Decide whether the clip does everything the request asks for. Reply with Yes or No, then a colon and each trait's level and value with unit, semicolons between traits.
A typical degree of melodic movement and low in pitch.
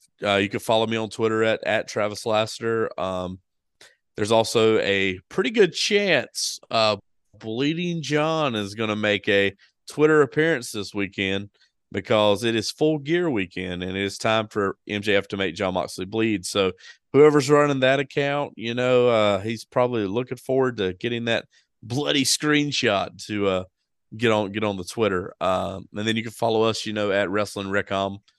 Yes: average, 3.9 semitones; low, 110 Hz